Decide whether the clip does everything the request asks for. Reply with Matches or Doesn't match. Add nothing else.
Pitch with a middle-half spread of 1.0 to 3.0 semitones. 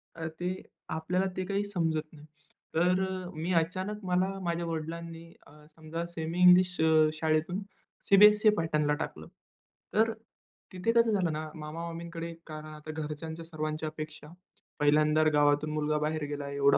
Matches